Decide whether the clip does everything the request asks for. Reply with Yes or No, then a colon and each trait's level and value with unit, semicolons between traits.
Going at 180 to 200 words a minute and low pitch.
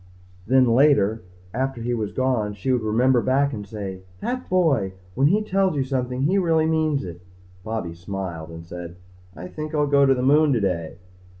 Yes: average, 185 wpm; low, 125 Hz